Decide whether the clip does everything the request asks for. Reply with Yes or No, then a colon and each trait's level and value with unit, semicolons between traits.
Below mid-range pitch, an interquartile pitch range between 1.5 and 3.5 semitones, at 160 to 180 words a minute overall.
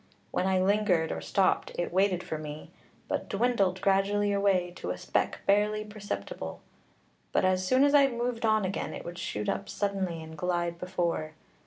No: high, 190 Hz; average, 2.9 semitones; average, 175 wpm